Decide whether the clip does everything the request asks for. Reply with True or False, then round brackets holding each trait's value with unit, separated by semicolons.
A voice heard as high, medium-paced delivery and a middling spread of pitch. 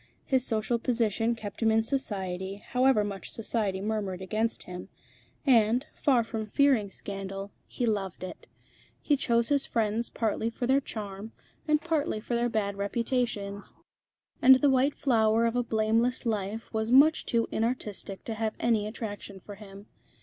True (225 Hz; 155 wpm; 3.0 semitones)